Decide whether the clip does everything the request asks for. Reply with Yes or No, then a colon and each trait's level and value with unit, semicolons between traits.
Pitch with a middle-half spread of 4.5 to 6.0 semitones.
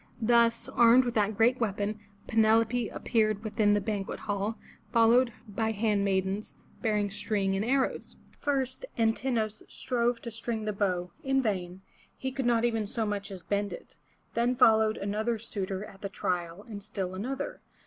No: narrow, 2.6 semitones